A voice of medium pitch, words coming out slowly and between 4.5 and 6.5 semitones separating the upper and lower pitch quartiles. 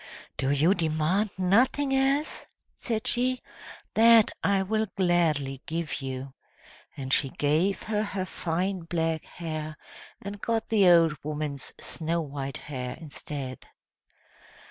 Yes: medium, 170 Hz; slow, 120 wpm; wide, 5.6 semitones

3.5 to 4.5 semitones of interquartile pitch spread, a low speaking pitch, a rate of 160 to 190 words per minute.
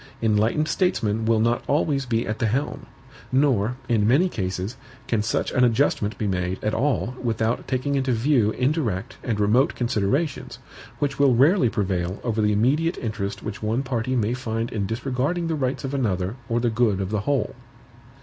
Yes: average, 4.1 semitones; low, 115 Hz; average, 180 wpm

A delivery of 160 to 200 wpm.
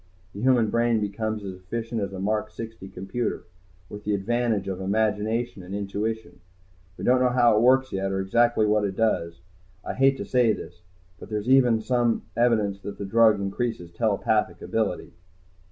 Yes: average, 175 wpm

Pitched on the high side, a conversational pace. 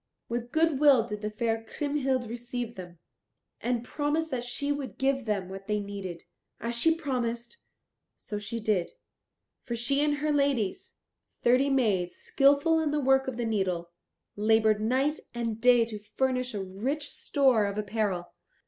Yes: high, 240 Hz; average, 160 wpm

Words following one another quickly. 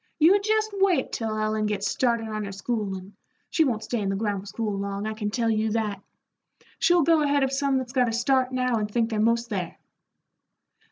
Yes: fast, 210 wpm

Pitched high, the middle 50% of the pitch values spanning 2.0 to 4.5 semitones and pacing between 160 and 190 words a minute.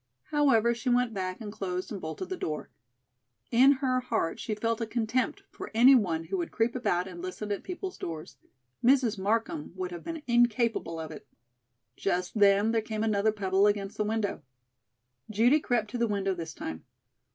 Yes: high, 215 Hz; average, 4.1 semitones; average, 185 wpm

